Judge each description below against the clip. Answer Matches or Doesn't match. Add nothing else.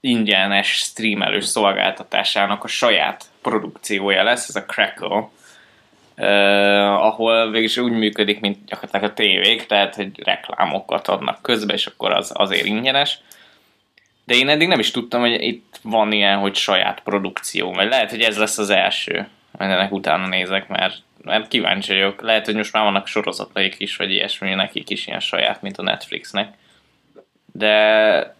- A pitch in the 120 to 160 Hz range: Doesn't match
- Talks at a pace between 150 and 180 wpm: Matches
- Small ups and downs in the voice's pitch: Matches